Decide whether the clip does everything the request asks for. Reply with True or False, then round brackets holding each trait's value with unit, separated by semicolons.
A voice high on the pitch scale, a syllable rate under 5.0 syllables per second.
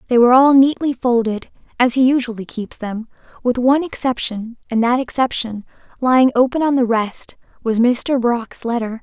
True (245 Hz; 4.6 syllables/s)